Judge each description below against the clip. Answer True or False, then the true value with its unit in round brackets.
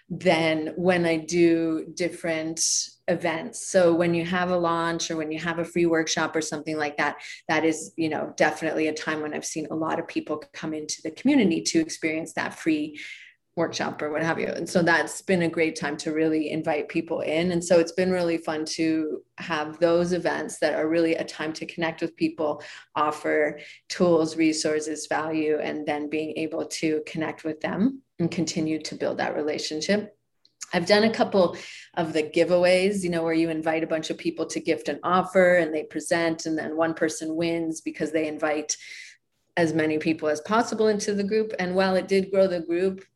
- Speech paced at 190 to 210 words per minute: True (200 wpm)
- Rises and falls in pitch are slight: True (2.1 semitones)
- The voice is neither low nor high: True (165 Hz)